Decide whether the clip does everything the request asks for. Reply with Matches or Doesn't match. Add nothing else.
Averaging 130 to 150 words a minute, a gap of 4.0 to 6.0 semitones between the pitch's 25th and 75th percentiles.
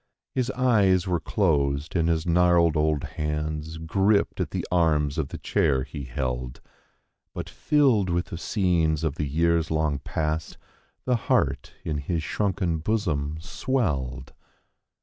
Doesn't match